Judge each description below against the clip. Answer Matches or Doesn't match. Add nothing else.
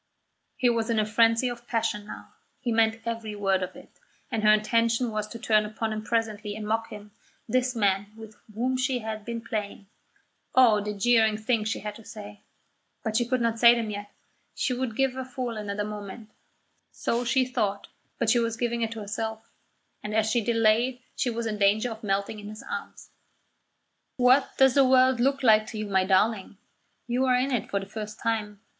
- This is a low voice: Doesn't match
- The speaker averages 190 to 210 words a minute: Matches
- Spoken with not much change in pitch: Matches